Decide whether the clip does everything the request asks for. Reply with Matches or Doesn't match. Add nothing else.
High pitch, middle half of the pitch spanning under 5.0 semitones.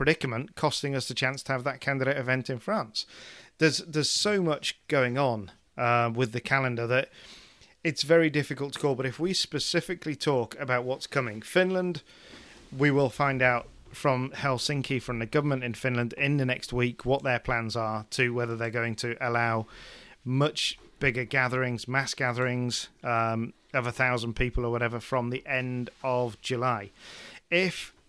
Doesn't match